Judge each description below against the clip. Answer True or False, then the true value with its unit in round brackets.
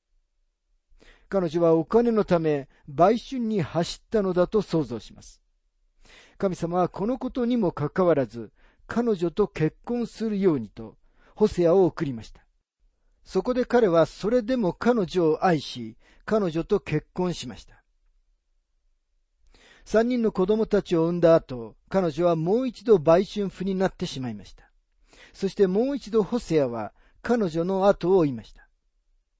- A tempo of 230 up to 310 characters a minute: True (270 characters per minute)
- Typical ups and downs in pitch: False (7.9 semitones)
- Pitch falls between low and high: True (175 Hz)